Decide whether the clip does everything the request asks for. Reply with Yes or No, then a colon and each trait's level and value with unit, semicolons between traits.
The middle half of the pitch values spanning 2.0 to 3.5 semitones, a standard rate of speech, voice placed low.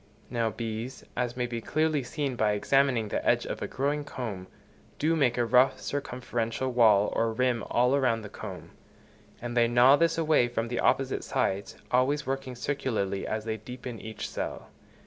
Yes: average, 3.0 semitones; average, 175 wpm; low, 120 Hz